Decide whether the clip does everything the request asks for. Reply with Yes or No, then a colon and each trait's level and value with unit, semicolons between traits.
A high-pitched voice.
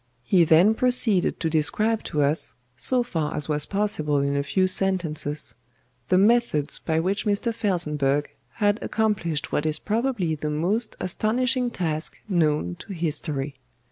No: medium, 175 Hz